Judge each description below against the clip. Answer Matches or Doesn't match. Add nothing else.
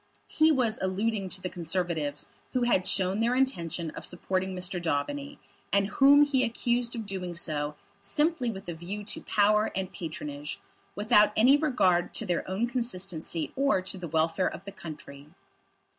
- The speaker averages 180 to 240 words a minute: Doesn't match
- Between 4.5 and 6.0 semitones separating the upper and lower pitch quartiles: Matches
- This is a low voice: Doesn't match